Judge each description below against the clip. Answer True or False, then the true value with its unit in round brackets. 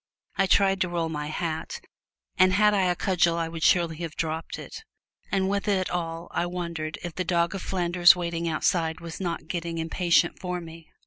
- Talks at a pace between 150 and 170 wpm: False (195 wpm)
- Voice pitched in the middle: True (170 Hz)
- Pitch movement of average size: False (1.9 semitones)